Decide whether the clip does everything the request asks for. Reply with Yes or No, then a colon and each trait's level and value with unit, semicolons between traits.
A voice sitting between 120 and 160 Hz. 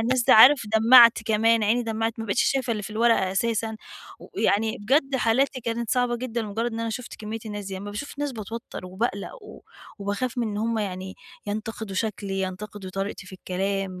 No: high, 220 Hz